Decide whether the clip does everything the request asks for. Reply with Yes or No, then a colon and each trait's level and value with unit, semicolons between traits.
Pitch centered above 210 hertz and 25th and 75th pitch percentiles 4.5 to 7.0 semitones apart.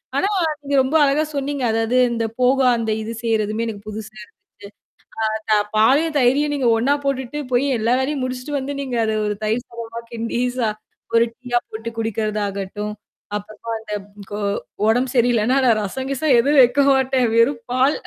No: high, 240 Hz; average, 3.2 semitones